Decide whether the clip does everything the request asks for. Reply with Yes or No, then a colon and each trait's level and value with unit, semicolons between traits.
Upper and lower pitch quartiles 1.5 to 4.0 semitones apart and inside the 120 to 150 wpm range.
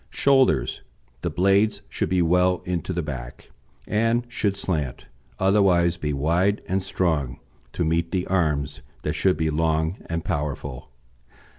Yes: average, 3.7 semitones; average, 140 wpm